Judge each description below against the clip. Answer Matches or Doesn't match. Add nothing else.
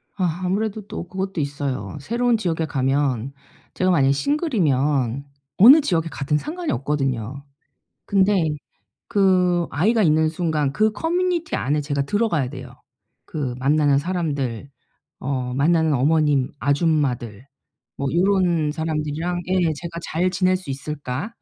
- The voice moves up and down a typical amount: Matches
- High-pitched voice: Doesn't match